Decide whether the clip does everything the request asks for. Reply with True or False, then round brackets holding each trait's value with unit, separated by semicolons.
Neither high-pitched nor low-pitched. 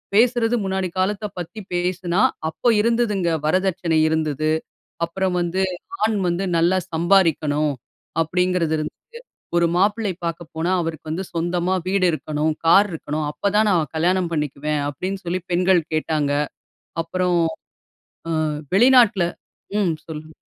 True (175 Hz)